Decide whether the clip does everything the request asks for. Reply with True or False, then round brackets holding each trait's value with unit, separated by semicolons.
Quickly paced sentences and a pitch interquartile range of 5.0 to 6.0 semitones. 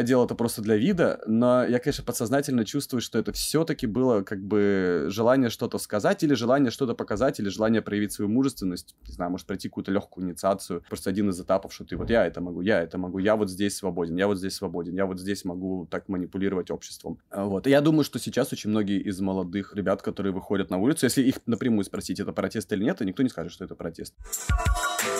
False (220 wpm; 4.1 semitones)